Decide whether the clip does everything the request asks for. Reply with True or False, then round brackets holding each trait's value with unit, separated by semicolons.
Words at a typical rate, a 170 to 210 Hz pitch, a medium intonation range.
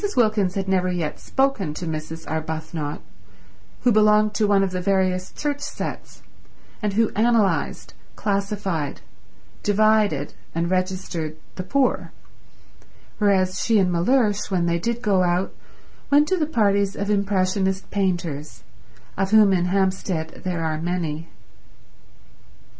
False (130 wpm; 190 Hz; 3.3 semitones)